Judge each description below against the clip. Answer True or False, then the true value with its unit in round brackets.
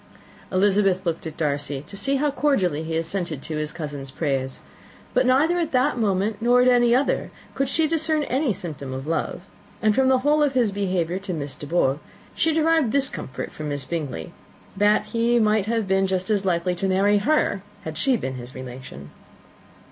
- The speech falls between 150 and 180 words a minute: False (195 wpm)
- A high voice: True (195 Hz)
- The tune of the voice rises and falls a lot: True (8.4 semitones)